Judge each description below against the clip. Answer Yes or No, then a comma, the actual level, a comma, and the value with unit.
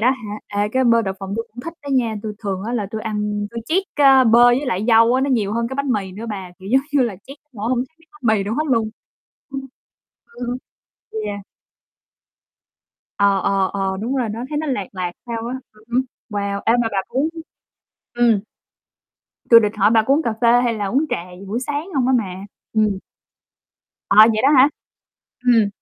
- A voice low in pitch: No, high, 230 Hz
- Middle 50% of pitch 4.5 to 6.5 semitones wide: No, average, 3.8 semitones